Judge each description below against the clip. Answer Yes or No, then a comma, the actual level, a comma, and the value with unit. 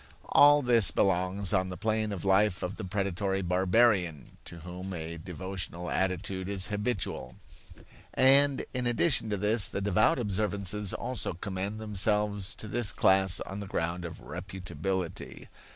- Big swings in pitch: No, narrow, 2.6 semitones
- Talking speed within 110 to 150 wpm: Yes, average, 145 wpm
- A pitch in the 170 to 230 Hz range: No, very low, 95 Hz